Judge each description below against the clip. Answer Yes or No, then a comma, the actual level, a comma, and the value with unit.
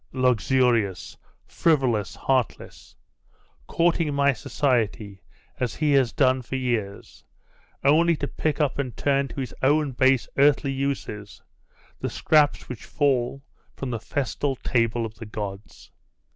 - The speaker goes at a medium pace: No, slow, 130 wpm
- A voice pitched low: Yes, low, 130 Hz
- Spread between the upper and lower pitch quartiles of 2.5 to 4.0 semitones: Yes, average, 3.4 semitones